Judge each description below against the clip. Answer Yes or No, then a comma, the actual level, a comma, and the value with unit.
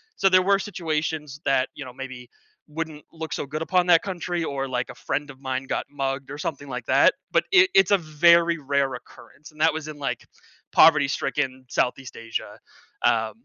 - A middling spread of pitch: Yes, average, 3.7 semitones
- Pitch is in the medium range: Yes, medium, 150 Hz